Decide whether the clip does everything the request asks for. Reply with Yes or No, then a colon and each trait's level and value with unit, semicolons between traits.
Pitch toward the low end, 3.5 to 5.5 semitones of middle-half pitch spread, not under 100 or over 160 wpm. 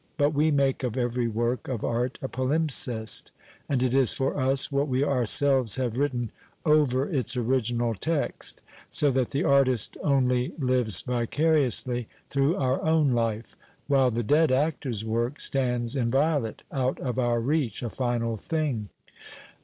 No: low, 130 Hz; average, 2.8 semitones; average, 155 wpm